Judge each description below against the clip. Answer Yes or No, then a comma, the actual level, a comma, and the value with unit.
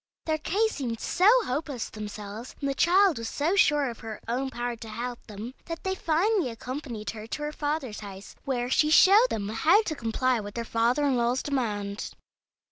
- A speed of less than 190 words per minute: No, average, 200 wpm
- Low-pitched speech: No, very high, 255 Hz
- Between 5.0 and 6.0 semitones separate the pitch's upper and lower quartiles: Yes, wide, 5.4 semitones